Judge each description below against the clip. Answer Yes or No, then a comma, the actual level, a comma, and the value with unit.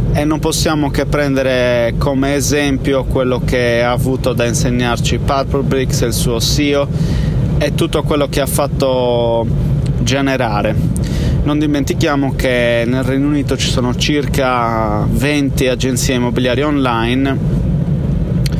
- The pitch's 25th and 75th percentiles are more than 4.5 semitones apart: No, average, 2.7 semitones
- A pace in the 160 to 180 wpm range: No, average, 125 wpm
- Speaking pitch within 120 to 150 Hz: Yes, low, 135 Hz